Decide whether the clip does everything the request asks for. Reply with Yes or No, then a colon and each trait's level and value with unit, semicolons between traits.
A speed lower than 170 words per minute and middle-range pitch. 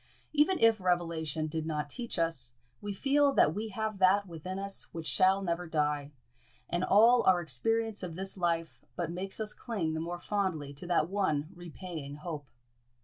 No: average, 175 wpm; medium, 175 Hz